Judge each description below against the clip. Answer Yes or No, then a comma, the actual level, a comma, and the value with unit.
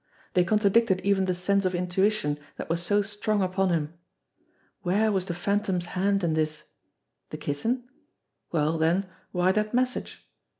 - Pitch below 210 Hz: Yes, high, 190 Hz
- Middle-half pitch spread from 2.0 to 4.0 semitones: Yes, average, 2.9 semitones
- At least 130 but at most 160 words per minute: Yes, average, 155 wpm